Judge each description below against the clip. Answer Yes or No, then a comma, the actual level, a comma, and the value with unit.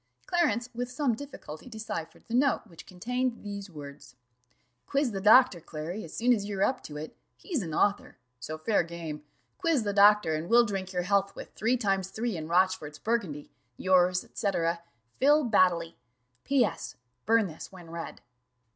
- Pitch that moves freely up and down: Yes, wide, 5.9 semitones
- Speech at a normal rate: Yes, average, 170 wpm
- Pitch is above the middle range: Yes, high, 200 Hz